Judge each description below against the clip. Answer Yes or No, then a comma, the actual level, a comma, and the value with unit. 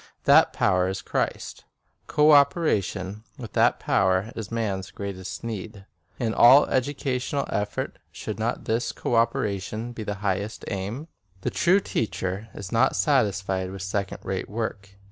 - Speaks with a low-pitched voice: Yes, low, 105 Hz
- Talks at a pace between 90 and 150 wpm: Yes, average, 145 wpm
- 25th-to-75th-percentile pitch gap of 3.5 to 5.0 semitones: Yes, average, 3.8 semitones